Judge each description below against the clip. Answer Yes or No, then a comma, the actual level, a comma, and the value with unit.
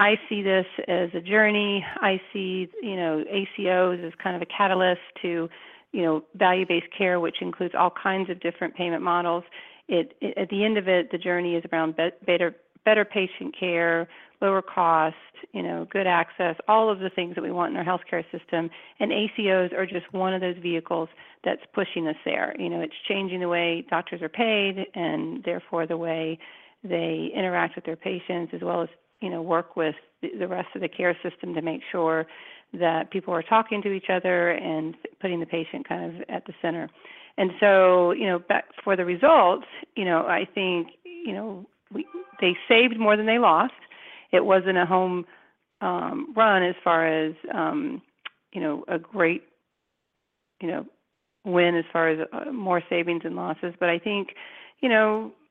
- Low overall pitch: No, medium, 180 Hz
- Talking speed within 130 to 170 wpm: No, average, 185 wpm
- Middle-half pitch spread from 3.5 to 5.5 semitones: No, average, 2.8 semitones